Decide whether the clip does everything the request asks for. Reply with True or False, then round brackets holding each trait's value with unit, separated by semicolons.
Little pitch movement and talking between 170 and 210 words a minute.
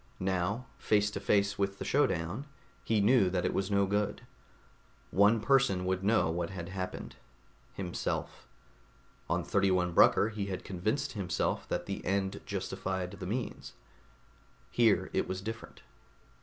False (2.3 semitones; 140 wpm)